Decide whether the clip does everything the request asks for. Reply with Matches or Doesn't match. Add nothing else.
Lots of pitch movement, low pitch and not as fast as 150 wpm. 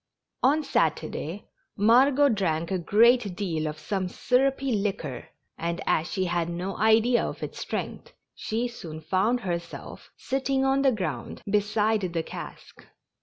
Doesn't match